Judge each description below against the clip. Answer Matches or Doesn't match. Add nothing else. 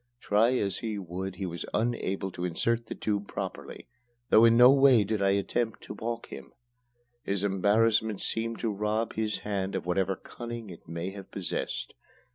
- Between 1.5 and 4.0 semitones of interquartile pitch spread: Matches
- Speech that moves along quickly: Doesn't match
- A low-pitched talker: Matches